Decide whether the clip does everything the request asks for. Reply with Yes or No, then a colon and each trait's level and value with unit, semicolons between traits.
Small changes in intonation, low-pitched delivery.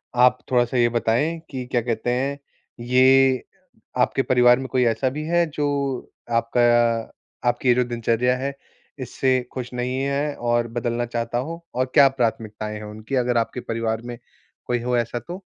Yes: narrow, 1.9 semitones; low, 125 Hz